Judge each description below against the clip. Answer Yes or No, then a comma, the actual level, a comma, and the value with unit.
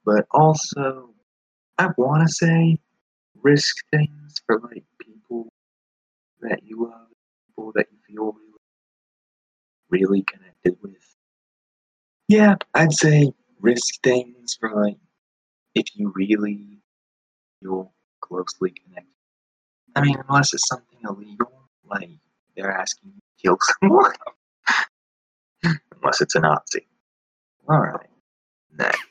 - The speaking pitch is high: No, low, 115 Hz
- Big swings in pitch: Yes, wide, 7.0 semitones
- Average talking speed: No, slow, 115 wpm